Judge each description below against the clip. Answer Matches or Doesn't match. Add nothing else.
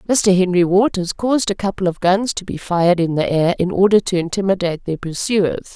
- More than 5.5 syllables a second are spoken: Matches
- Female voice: Matches